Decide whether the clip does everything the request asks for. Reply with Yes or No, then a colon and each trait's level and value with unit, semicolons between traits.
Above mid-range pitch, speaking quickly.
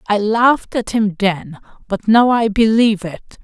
No: high, 215 Hz; average, 175 wpm